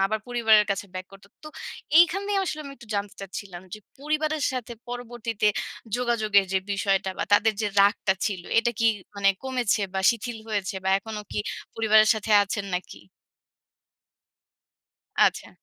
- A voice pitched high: Yes, high, 220 Hz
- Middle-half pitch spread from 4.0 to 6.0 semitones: No, average, 3.3 semitones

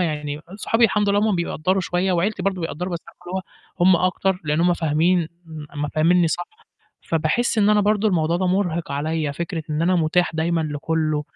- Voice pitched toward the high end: No, medium, 170 Hz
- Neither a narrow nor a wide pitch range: Yes, average, 3.2 semitones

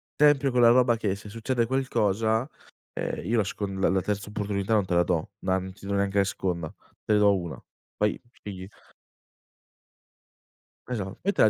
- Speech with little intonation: No, average, 3.1 semitones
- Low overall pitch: Yes, low, 105 Hz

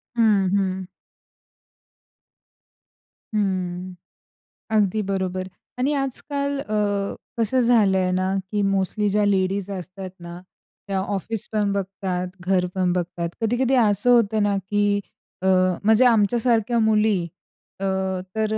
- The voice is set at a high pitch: Yes, high, 200 Hz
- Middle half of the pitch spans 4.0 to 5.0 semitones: No, average, 2.8 semitones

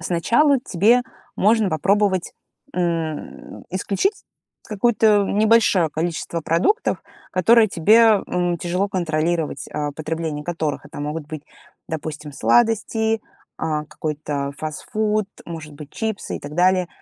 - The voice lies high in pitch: No, medium, 175 Hz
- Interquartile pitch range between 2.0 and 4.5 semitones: No, average, 5.3 semitones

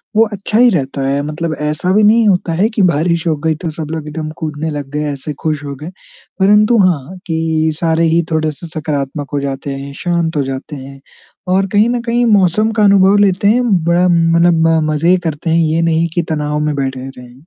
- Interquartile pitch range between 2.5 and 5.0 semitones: Yes, average, 3.7 semitones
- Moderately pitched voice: Yes, medium, 160 Hz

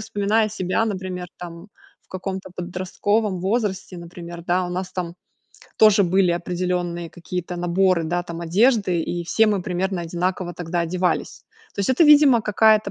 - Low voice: No, medium, 185 Hz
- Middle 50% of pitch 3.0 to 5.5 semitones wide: No, narrow, 2.6 semitones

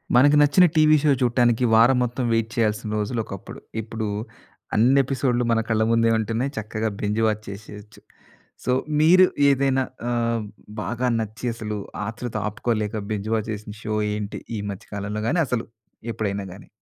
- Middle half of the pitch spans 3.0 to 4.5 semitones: No, narrow, 2.6 semitones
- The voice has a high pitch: No, low, 115 Hz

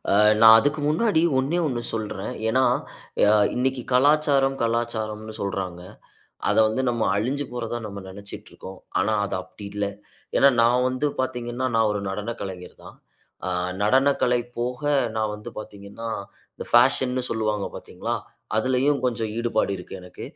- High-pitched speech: No, low, 115 Hz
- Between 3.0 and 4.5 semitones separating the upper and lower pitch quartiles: Yes, average, 3.7 semitones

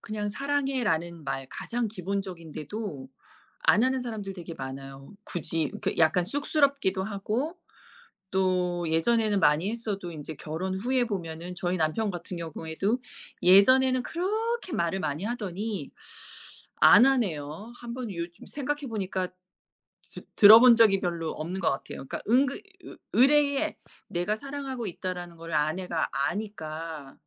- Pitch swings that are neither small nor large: No, wide, 6.2 semitones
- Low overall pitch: No, high, 195 Hz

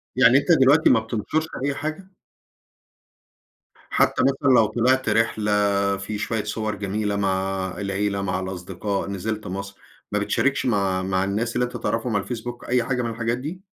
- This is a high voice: No, low, 110 Hz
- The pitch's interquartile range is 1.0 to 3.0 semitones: No, average, 4.2 semitones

